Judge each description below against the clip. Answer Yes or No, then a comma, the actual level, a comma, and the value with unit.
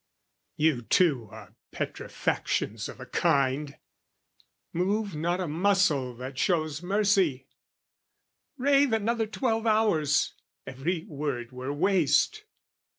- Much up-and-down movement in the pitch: Yes, wide, 6.7 semitones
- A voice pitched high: No, medium, 165 Hz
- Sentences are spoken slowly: Yes, slow, 100 wpm